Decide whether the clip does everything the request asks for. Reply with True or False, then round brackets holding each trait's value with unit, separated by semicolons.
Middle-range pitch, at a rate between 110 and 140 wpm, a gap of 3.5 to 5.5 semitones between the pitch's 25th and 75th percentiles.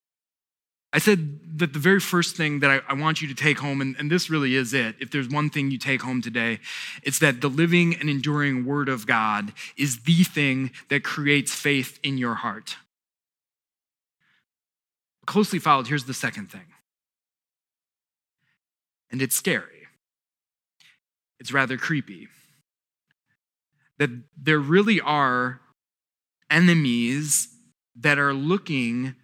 False (145 Hz; 135 wpm; 2.7 semitones)